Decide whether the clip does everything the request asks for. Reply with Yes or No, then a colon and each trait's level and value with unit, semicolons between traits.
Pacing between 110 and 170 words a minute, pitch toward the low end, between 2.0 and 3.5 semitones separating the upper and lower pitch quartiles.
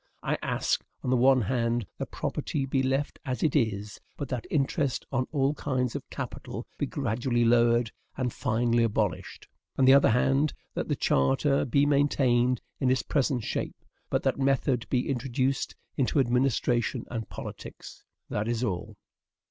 Yes: average, 160 wpm; low, 125 Hz; narrow, 2.5 semitones